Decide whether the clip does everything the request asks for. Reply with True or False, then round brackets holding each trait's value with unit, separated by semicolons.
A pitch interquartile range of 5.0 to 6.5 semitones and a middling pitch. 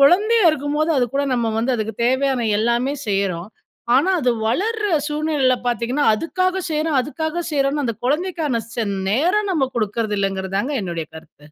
False (5.5 semitones; 270 Hz)